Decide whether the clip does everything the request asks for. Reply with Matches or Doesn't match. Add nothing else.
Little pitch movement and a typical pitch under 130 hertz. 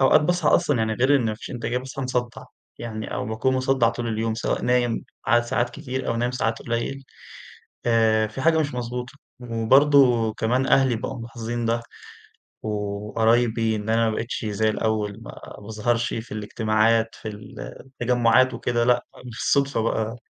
Matches